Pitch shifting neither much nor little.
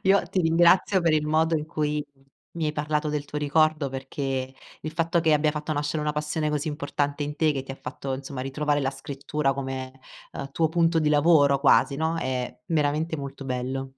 No: narrow, 2.3 semitones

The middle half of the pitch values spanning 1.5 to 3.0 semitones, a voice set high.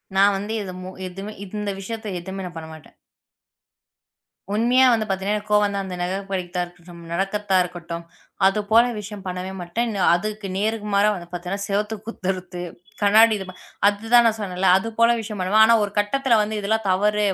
Yes: narrow, 2.6 semitones; high, 200 Hz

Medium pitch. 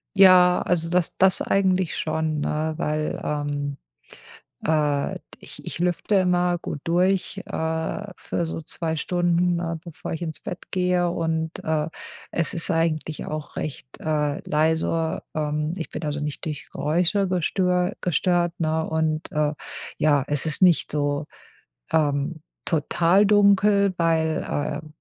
Yes: medium, 160 Hz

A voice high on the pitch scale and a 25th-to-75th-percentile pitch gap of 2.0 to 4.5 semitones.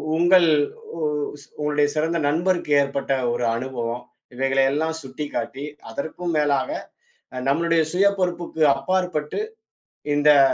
No: medium, 150 Hz; average, 3.6 semitones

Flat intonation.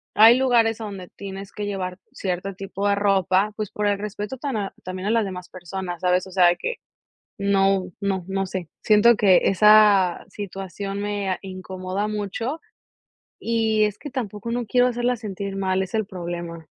Yes: narrow, 2.3 semitones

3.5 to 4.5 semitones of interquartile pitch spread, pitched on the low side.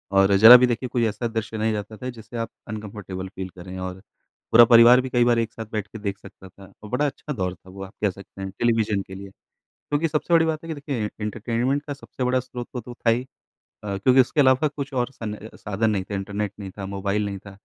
Yes: average, 4.1 semitones; low, 110 Hz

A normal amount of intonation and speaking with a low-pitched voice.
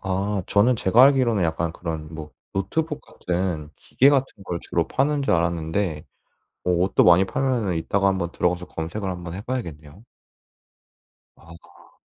Yes: average, 4.7 semitones; very low, 95 Hz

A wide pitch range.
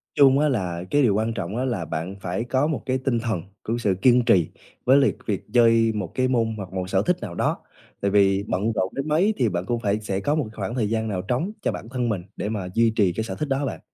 No: average, 4.8 semitones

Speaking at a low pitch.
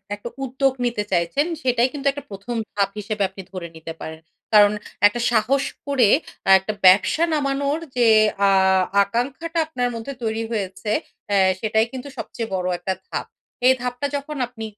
No: high, 230 Hz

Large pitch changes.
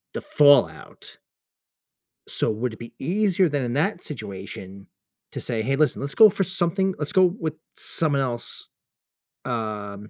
Yes: wide, 7.8 semitones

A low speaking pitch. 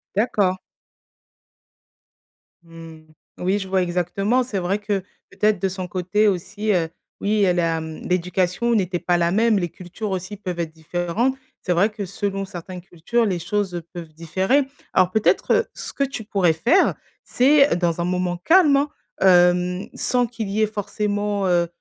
No: high, 190 Hz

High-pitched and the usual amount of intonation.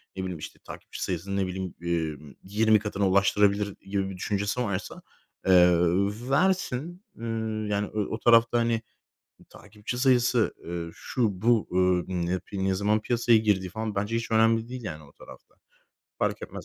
No: low, 105 Hz; average, 3.4 semitones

